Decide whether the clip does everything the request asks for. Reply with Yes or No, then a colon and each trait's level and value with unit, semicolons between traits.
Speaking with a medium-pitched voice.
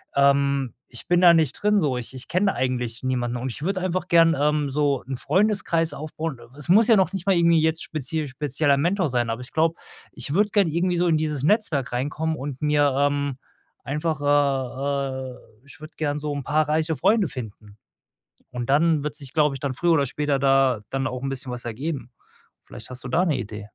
Yes: medium, 145 Hz